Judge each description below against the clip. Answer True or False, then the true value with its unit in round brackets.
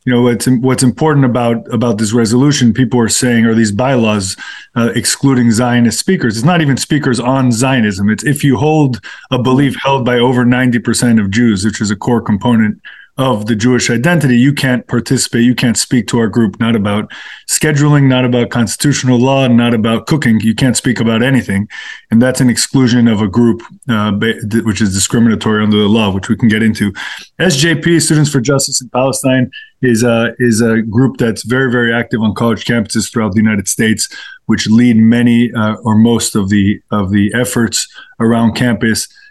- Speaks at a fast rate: False (190 wpm)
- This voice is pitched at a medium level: False (120 Hz)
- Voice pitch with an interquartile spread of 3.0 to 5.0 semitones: False (2.4 semitones)